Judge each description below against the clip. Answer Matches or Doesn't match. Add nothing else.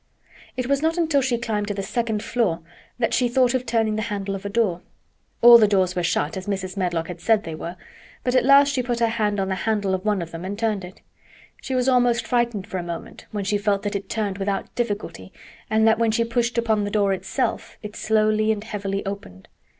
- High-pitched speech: Matches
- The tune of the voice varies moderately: Matches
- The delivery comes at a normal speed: Doesn't match